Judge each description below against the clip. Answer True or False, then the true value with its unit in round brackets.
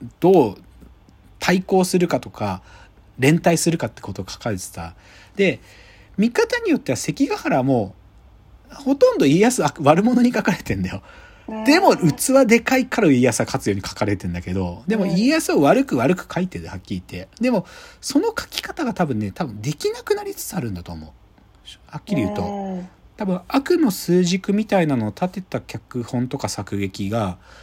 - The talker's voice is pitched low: False (165 Hz)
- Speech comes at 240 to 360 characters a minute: True (335 characters per minute)